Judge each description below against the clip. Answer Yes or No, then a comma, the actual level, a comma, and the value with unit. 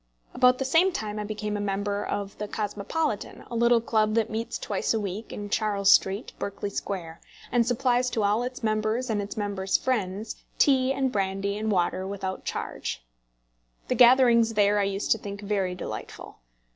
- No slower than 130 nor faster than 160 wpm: No, average, 180 wpm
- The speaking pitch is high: Yes, high, 210 Hz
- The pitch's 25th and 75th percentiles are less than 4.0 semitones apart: Yes, average, 2.9 semitones